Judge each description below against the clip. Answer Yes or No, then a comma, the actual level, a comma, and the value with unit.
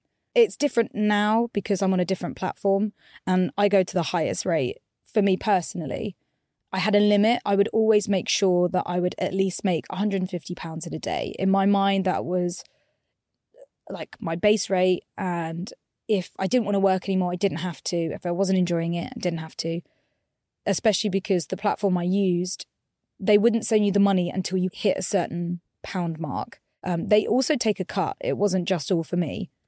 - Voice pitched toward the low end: No, high, 190 Hz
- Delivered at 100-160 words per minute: No, average, 200 wpm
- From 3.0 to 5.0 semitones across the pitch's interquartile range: No, narrow, 2.5 semitones